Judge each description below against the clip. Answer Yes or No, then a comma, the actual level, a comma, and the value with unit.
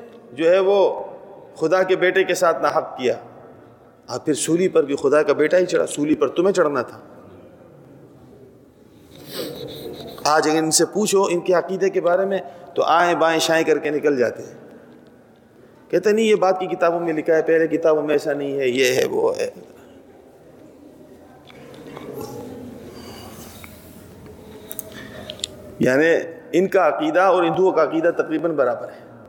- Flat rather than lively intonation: No, average, 3.6 semitones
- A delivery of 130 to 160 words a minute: Yes, average, 155 wpm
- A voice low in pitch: No, medium, 170 Hz